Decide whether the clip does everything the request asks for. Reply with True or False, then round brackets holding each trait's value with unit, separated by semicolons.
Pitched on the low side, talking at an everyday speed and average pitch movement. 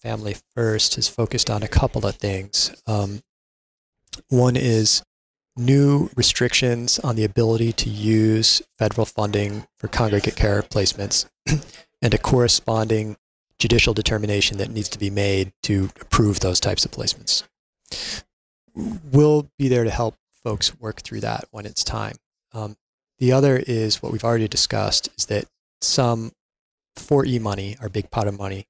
True (110 Hz; 150 wpm; 3.0 semitones)